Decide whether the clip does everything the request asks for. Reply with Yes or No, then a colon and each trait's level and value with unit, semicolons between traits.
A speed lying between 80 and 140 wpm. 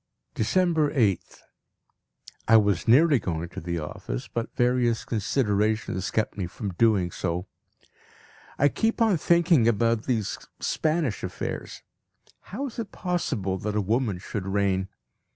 Yes: slow, 135 wpm